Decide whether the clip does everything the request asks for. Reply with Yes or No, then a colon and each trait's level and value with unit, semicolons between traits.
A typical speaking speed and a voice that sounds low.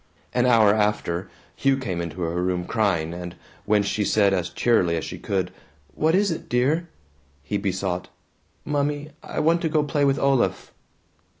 Yes: average, 170 wpm; low, 105 Hz